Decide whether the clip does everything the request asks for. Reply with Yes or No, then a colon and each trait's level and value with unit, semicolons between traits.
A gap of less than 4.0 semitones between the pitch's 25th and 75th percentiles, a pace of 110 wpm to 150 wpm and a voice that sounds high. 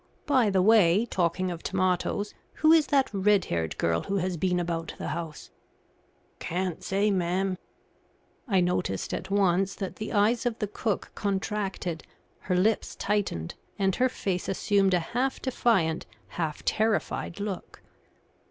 Yes: average, 3.0 semitones; average, 145 wpm; high, 195 Hz